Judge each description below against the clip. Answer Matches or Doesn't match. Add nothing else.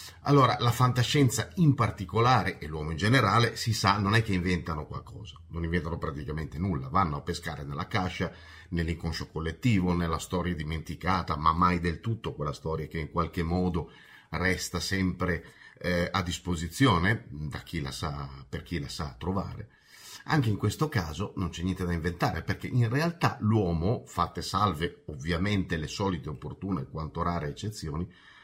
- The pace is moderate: Matches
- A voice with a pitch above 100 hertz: Doesn't match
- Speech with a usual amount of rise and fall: Matches